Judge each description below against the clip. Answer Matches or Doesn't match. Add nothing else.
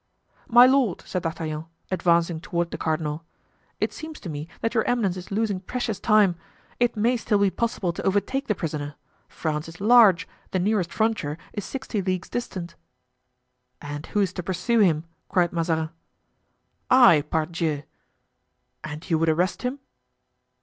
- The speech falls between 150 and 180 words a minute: Matches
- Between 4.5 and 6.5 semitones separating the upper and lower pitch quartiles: Matches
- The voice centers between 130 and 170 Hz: Doesn't match